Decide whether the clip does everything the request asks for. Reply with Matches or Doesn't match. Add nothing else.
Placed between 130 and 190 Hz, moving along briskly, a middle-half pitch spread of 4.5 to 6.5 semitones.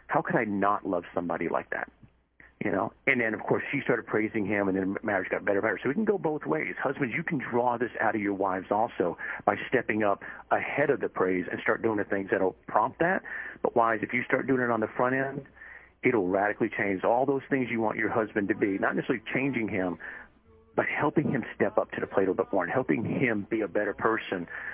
Doesn't match